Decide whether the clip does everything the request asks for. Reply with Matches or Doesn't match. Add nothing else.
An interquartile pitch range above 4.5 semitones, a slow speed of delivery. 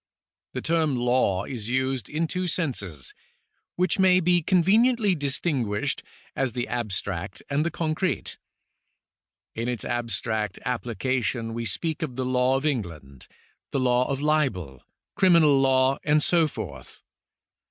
Matches